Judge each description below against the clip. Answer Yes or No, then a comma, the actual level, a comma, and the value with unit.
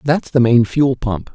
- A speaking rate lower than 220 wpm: No, fast, 225 wpm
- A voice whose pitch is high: No, low, 125 Hz